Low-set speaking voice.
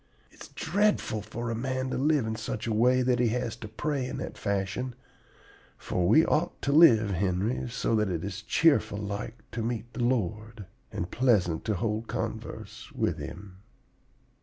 Yes: low, 115 Hz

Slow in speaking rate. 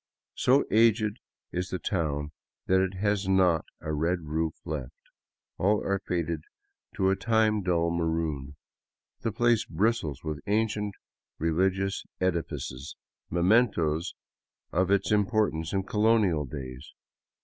Yes: slow, 125 wpm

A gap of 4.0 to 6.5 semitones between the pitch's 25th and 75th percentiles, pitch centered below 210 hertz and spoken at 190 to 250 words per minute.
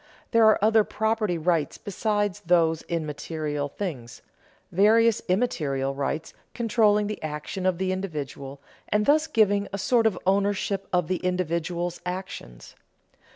No: average, 4.7 semitones; medium, 185 Hz; slow, 135 wpm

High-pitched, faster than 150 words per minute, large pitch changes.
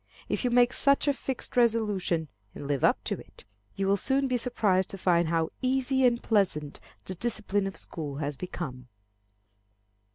Yes: high, 195 Hz; average, 170 wpm; wide, 6.6 semitones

